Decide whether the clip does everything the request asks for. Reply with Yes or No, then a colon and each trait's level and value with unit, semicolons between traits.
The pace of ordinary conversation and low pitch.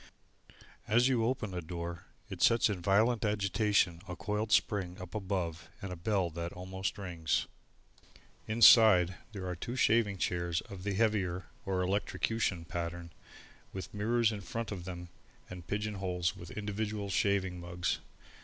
Yes: average, 150 wpm; very low, 95 Hz